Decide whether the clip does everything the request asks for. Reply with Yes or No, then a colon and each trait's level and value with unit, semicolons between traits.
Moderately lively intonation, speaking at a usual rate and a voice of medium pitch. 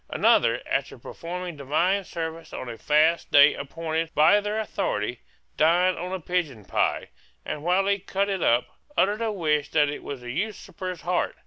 Yes: average, 4.1 semitones; average, 175 wpm; medium, 165 Hz